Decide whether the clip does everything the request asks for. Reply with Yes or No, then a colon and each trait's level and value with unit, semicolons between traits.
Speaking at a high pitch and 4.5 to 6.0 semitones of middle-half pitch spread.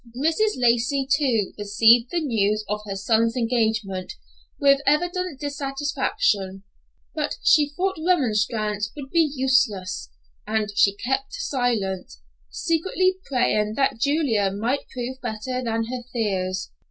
Yes: high, 245 Hz; average, 5.1 semitones